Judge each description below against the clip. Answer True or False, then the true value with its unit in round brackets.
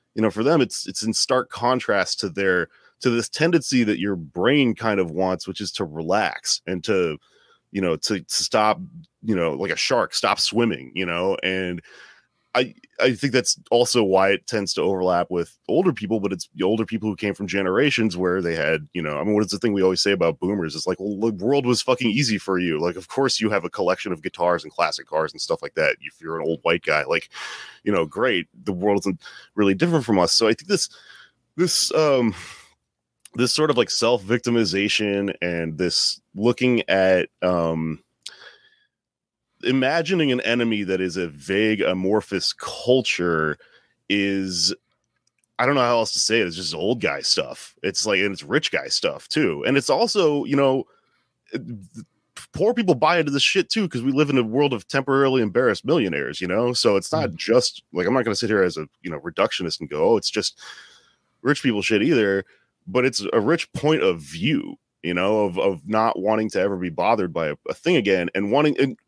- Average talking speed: False (210 wpm)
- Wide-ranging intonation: True (5.7 semitones)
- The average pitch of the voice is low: True (105 Hz)